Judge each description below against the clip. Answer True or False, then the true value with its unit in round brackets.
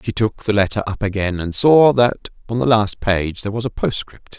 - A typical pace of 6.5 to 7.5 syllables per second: False (5.4 syllables/s)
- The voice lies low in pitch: True (105 Hz)